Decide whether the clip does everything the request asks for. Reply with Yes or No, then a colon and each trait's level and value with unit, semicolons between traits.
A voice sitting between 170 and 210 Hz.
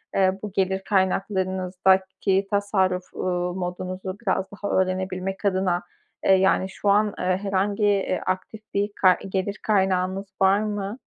Yes: high, 190 Hz